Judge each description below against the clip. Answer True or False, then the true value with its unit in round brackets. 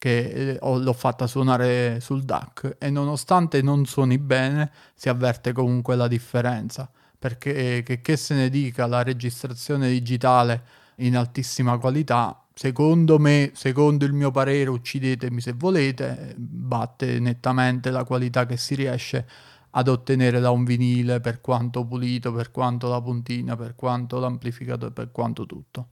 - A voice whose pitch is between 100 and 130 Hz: True (125 Hz)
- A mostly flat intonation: True (1.8 semitones)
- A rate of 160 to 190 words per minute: False (145 wpm)